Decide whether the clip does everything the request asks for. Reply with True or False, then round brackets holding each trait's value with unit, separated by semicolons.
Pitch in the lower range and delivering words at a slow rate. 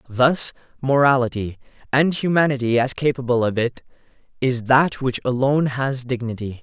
True (130 Hz; 125 wpm)